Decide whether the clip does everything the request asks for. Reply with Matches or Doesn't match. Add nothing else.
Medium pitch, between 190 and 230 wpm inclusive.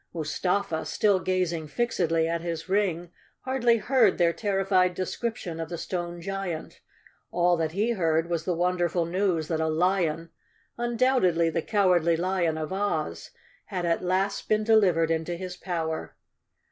Doesn't match